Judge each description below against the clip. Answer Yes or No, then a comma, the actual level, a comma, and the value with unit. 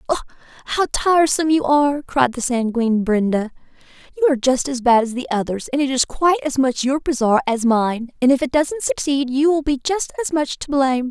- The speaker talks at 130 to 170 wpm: No, fast, 205 wpm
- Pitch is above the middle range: Yes, very high, 270 Hz